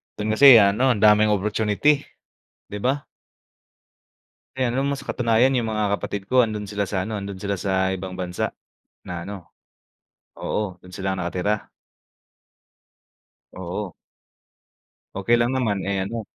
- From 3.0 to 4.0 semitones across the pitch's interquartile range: Yes, average, 3.5 semitones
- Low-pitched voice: Yes, low, 105 Hz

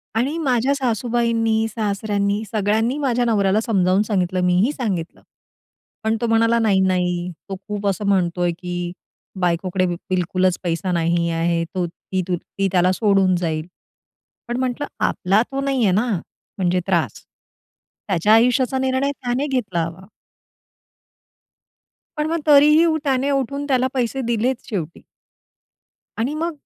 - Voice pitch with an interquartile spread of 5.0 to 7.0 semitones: Yes, wide, 5.6 semitones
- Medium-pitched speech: No, high, 210 Hz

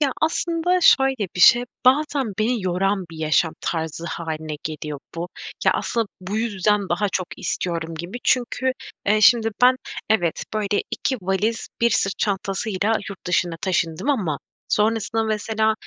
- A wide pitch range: No, average, 4.9 semitones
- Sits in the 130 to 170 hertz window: No, high, 205 Hz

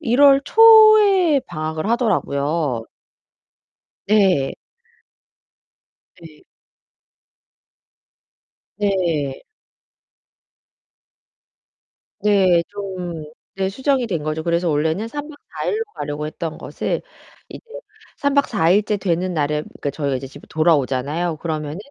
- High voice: No, medium, 175 Hz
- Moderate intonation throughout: No, wide, 6.4 semitones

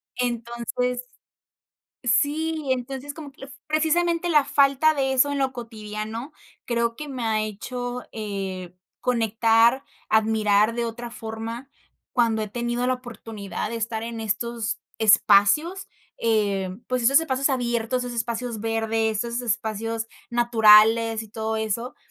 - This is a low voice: No, high, 235 Hz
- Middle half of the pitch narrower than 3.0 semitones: Yes, narrow, 2.5 semitones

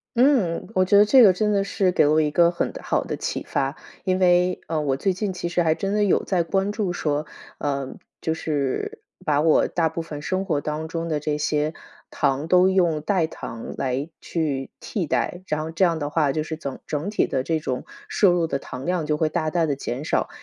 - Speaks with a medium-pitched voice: Yes, medium, 165 Hz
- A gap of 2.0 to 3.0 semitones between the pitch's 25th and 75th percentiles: No, average, 3.7 semitones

